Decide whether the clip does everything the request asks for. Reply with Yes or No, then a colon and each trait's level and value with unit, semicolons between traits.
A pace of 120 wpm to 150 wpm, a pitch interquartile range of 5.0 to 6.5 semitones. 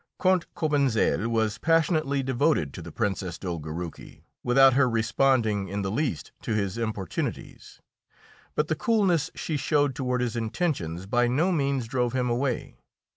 Yes: average, 145 wpm; wide, 5.4 semitones